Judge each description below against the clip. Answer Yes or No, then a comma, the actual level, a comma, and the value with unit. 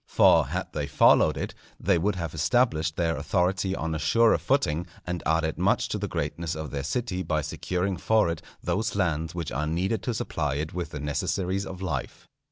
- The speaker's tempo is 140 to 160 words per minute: No, average, 195 wpm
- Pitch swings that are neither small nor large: Yes, average, 3.5 semitones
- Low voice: Yes, very low, 85 Hz